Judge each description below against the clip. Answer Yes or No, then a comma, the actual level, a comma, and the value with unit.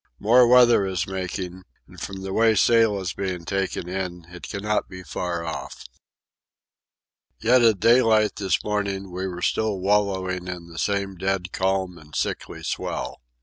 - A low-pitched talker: Yes, very low, 95 Hz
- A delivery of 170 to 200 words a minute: No, average, 155 wpm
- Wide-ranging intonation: No, narrow, 2.4 semitones